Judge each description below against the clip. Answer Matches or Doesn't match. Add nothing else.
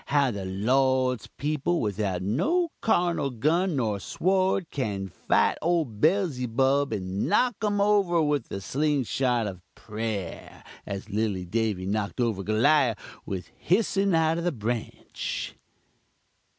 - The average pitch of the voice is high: Doesn't match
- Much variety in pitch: Matches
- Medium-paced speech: Doesn't match